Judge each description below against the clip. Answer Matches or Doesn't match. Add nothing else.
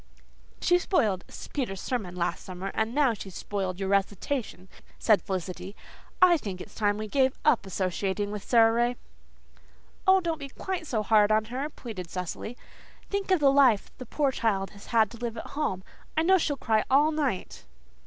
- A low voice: Doesn't match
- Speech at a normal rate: Matches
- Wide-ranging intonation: Matches